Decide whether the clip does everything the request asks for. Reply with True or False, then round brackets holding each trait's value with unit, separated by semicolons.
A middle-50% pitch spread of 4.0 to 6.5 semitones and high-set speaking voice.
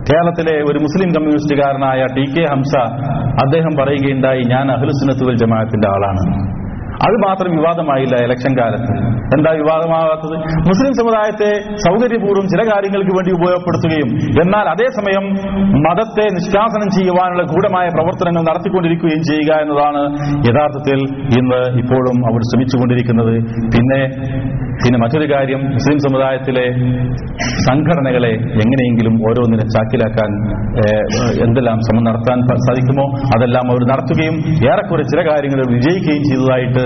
False (4.9 semitones; 135 Hz)